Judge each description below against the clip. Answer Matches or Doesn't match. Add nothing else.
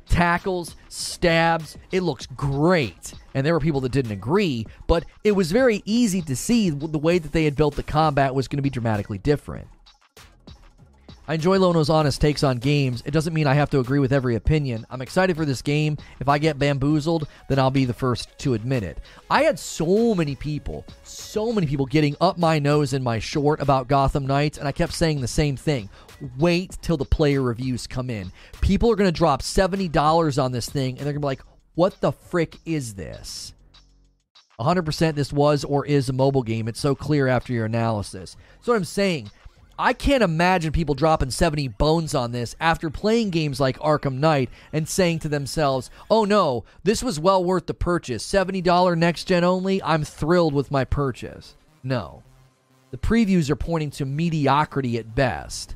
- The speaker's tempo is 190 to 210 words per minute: Matches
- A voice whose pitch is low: Doesn't match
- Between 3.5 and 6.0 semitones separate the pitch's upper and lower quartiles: Matches